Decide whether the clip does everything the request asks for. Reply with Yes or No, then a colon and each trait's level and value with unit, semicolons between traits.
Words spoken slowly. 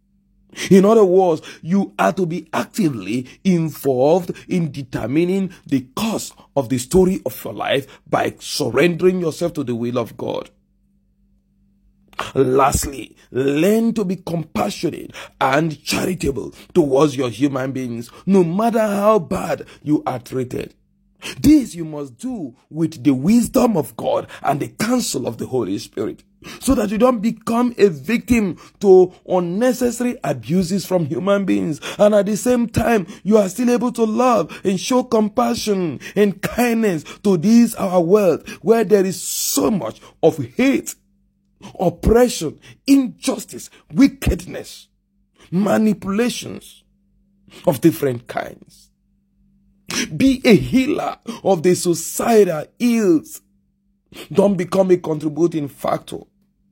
Yes: slow, 125 wpm